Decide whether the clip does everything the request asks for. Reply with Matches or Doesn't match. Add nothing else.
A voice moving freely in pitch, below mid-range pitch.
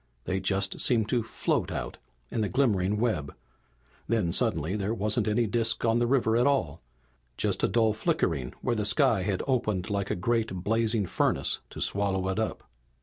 Doesn't match